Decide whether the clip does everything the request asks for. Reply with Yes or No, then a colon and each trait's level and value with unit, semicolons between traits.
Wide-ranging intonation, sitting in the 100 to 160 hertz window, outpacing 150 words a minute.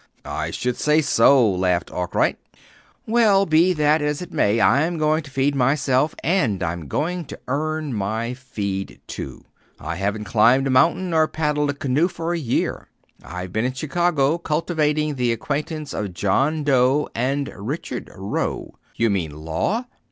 Yes: wide, 6.2 semitones; medium, 140 Hz; average, 160 wpm